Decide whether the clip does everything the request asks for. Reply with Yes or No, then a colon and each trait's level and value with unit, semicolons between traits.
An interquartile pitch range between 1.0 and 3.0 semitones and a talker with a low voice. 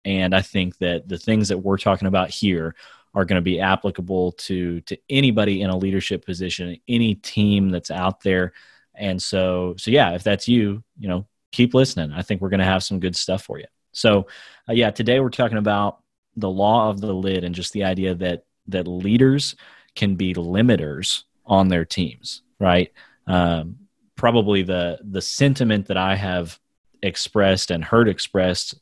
Yes: average, 2.7 semitones; very low, 95 Hz